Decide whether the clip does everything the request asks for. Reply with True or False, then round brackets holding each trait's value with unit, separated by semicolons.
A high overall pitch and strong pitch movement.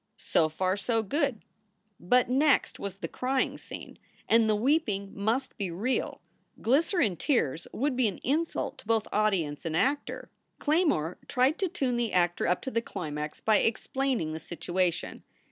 True (225 Hz; 6.6 semitones)